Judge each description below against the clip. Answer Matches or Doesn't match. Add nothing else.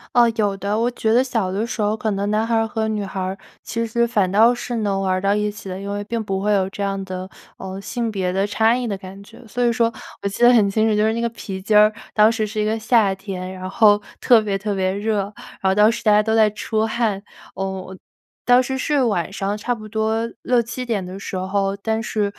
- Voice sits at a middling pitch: Doesn't match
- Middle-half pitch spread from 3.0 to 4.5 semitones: Doesn't match